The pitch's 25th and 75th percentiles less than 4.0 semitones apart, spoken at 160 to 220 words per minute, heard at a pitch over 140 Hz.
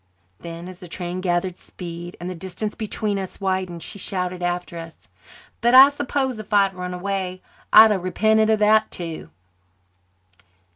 Yes: average, 3.3 semitones; average, 165 wpm; medium, 185 Hz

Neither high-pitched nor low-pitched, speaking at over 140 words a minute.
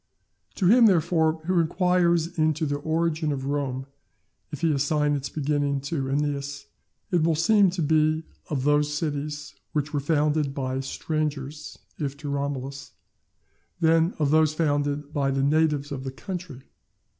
Yes: medium, 150 Hz; average, 150 wpm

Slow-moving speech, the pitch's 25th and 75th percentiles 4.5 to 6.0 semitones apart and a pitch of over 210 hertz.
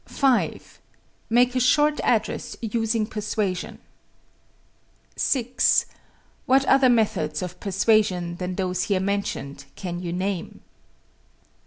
No: slow, 105 wpm; average, 4.8 semitones; high, 205 Hz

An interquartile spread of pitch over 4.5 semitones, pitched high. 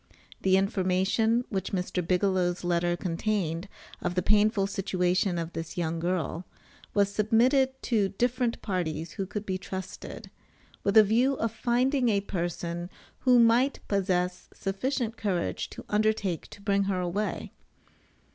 No: average, 3.6 semitones; high, 195 Hz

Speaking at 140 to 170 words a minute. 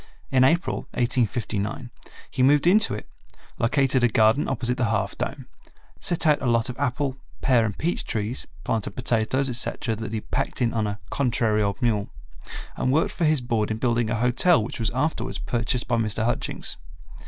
No: average, 185 wpm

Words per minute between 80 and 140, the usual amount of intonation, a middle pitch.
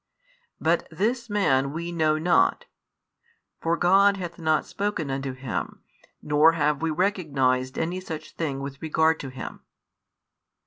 Yes: slow, 135 wpm; average, 4.2 semitones; medium, 160 Hz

